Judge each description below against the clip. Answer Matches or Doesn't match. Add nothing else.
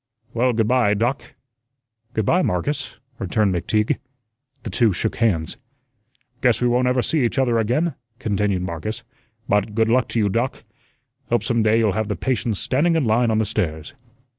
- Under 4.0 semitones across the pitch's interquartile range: Matches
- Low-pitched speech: Matches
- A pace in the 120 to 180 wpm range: Matches